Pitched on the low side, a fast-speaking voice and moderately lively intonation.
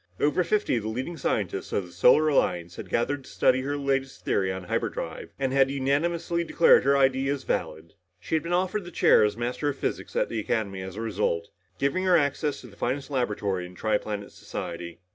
No: low, 130 Hz; fast, 215 wpm; wide, 6.0 semitones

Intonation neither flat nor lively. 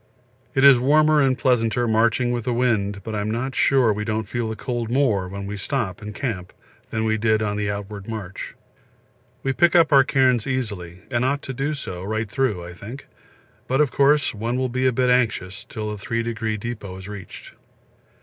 Yes: average, 4.0 semitones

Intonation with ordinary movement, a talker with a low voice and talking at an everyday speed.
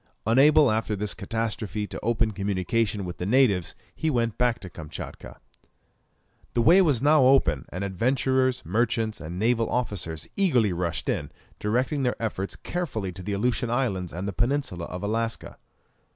Yes: average, 4.5 semitones; low, 110 Hz; average, 155 wpm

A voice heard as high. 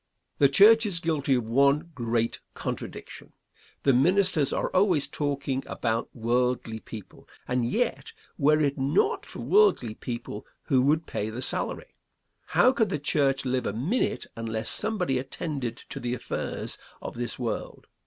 No: low, 135 Hz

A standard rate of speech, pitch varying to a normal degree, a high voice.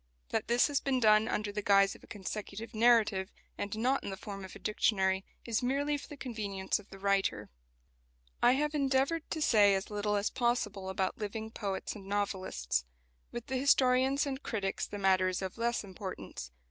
Yes: average, 190 wpm; average, 4.2 semitones; high, 210 Hz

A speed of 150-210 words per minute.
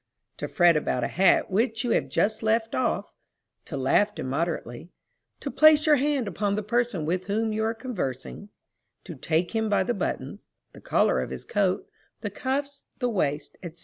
Yes: average, 180 wpm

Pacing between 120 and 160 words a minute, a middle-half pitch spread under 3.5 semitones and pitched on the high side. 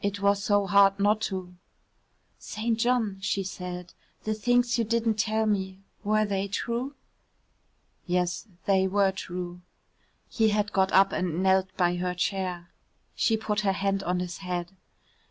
Yes: average, 155 wpm; average, 2.7 semitones; high, 195 Hz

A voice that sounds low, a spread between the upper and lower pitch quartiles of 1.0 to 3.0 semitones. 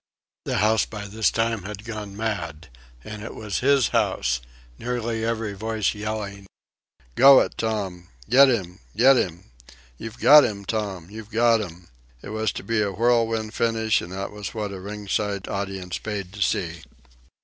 Yes: low, 105 Hz; narrow, 2.4 semitones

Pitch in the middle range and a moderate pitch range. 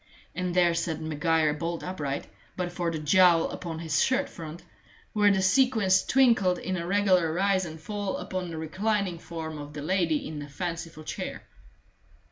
Yes: medium, 175 Hz; average, 3.0 semitones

